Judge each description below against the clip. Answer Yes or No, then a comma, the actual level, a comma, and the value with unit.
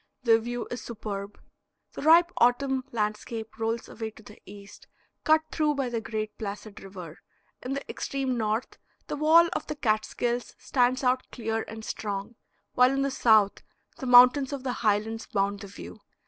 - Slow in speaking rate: No, average, 170 wpm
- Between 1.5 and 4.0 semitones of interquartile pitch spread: Yes, average, 3.4 semitones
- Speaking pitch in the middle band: No, high, 230 Hz